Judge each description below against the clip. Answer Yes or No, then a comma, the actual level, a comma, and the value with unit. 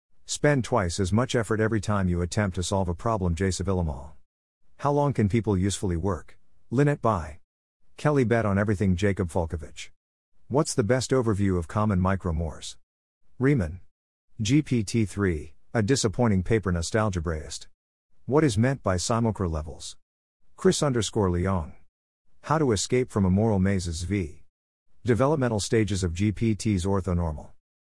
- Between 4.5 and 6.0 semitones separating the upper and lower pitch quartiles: Yes, average, 4.8 semitones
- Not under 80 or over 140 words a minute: Yes, slow, 135 wpm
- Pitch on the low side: Yes, low, 100 Hz